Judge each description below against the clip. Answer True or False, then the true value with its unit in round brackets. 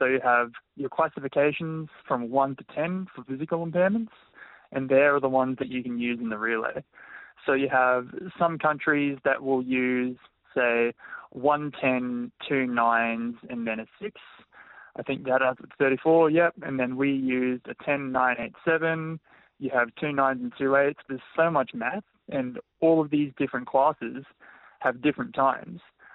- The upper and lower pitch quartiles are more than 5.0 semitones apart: False (3.9 semitones)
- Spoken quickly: False (175 wpm)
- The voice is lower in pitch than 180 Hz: True (135 Hz)